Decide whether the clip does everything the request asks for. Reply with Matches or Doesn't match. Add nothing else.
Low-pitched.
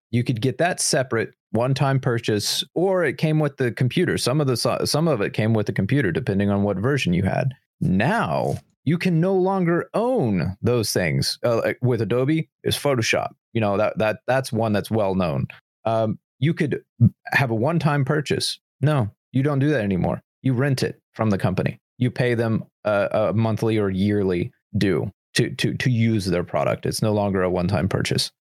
Matches